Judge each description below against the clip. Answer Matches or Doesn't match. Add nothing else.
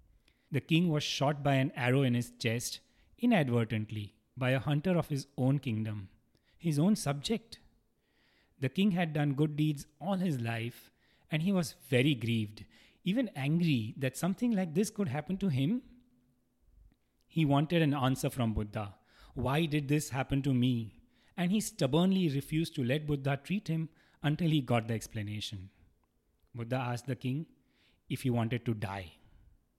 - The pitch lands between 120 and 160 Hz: Matches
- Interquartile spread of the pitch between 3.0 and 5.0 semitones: Doesn't match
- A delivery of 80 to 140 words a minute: Doesn't match